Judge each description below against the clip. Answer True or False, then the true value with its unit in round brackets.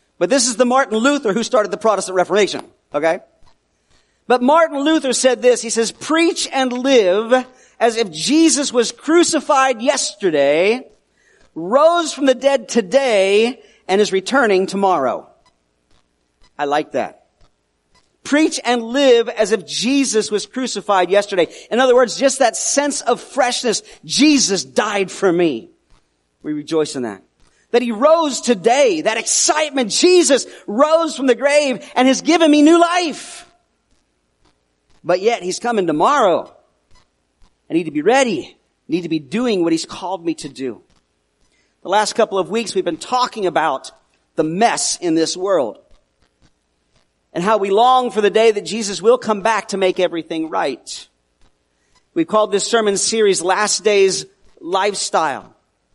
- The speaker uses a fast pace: False (150 wpm)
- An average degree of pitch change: False (6.7 semitones)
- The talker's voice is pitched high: True (220 Hz)